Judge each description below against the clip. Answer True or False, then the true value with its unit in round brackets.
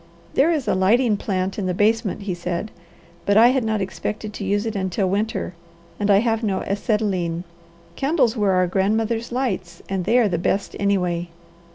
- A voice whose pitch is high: True (205 Hz)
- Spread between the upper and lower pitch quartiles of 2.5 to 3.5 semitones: True (3.1 semitones)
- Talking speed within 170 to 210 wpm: True (185 wpm)